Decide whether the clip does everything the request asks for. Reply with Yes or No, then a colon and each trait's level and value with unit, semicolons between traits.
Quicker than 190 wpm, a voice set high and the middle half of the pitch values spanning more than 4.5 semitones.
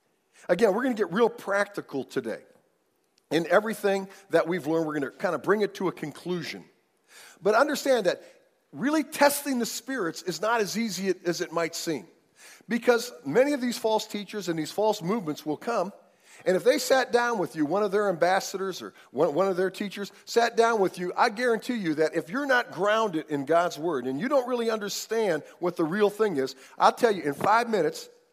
Yes: fast, 205 wpm; high, 205 Hz; wide, 5.5 semitones